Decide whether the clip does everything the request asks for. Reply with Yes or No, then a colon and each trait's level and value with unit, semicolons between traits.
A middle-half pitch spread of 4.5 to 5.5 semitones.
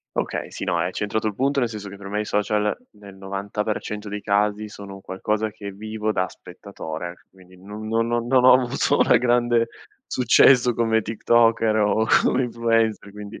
No: narrow, 2.4 semitones